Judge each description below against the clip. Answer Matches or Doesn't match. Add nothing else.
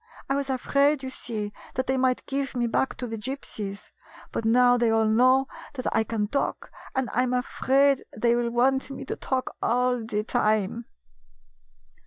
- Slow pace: Doesn't match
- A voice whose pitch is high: Matches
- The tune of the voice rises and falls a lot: Doesn't match